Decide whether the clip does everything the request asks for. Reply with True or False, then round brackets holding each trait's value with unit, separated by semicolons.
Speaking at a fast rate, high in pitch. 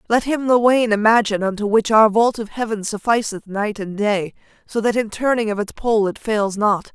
True (215 wpm; 215 Hz)